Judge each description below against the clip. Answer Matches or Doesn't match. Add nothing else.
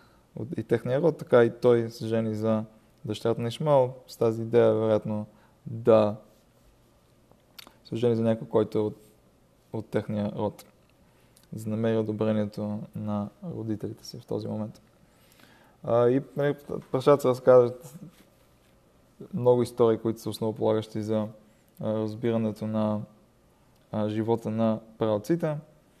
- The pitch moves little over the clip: Matches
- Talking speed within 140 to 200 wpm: Doesn't match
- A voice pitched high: Doesn't match